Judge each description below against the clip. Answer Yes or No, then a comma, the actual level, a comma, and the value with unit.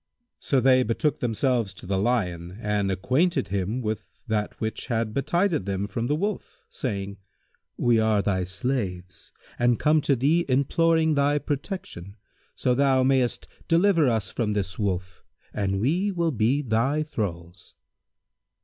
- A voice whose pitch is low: Yes, low, 115 Hz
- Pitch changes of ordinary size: No, wide, 6.2 semitones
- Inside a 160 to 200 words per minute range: No, average, 145 wpm